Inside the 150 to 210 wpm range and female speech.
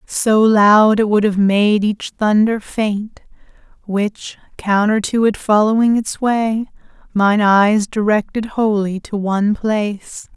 No: slow, 135 wpm; female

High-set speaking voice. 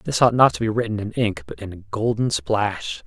No: low, 100 Hz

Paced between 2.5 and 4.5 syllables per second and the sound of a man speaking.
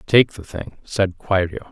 Yes: 4.0 syllables/s; male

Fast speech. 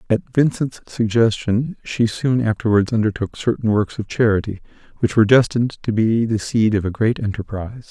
No: average, 165 wpm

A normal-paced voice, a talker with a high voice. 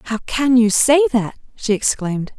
Yes: average, 175 wpm; high, 225 Hz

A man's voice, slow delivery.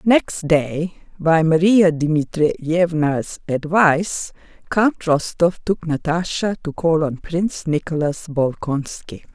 No: female; slow, 105 wpm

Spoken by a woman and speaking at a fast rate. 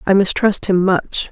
No: female; average, 185 wpm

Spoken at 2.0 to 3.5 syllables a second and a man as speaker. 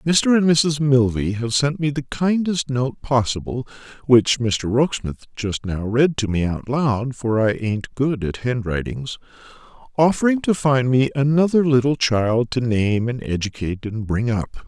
Yes: 3.4 syllables/s; male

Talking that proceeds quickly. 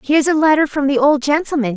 Yes: fast, 240 wpm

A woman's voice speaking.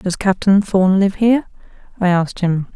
Yes: female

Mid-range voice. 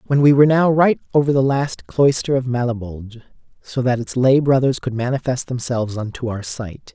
No: low, 130 Hz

